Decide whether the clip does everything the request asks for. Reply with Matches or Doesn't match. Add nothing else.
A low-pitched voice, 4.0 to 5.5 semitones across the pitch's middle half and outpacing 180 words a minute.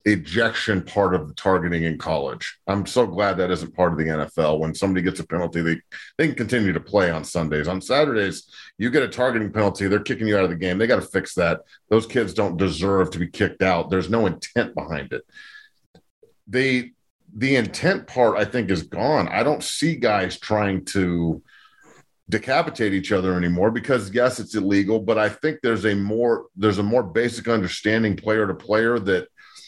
Matches